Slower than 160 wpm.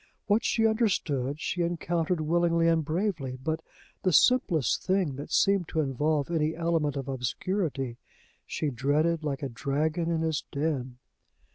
Yes: average, 145 wpm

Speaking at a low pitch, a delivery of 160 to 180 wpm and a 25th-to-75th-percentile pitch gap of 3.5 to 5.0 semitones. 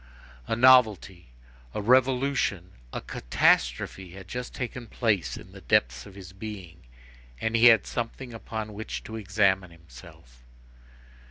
No: low, 105 Hz; slow, 135 wpm; average, 4.7 semitones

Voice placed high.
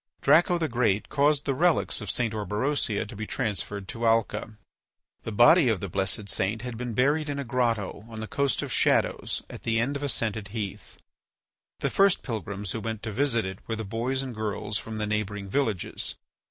No: low, 115 Hz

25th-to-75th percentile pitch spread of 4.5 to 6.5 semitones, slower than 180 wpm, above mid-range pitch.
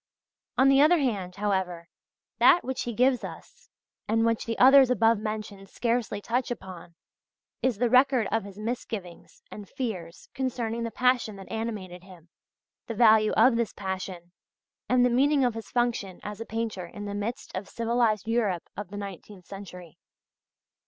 No: average, 3.8 semitones; average, 165 wpm; high, 220 Hz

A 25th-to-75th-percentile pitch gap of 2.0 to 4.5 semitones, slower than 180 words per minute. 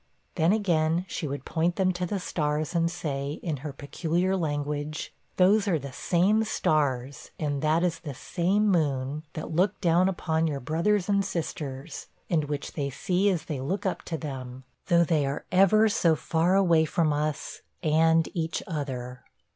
Yes: average, 3.6 semitones; average, 170 wpm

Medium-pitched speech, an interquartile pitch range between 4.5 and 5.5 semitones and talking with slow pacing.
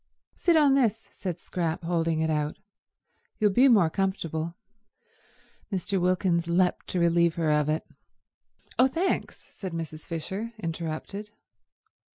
No: medium, 175 Hz; average, 3.8 semitones; slow, 130 wpm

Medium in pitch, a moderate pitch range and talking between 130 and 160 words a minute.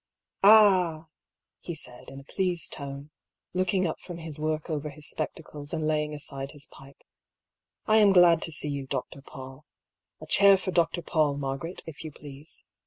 No: medium, 155 Hz; average, 3.5 semitones; average, 185 wpm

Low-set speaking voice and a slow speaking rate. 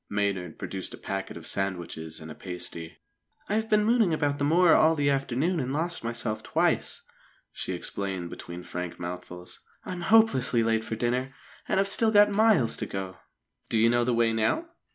No: low, 120 Hz; average, 180 wpm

